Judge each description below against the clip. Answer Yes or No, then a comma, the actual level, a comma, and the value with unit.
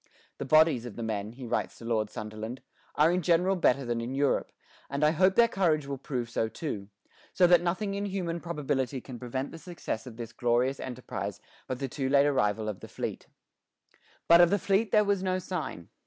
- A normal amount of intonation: No, wide, 6.6 semitones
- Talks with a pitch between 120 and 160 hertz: Yes, medium, 140 Hz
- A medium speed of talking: No, fast, 210 wpm